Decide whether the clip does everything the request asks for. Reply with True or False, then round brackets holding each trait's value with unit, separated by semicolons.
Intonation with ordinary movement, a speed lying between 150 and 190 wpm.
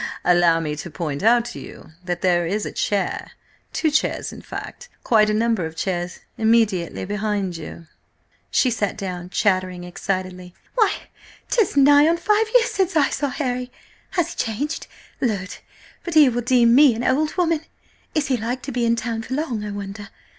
False (7.0 semitones; 175 wpm)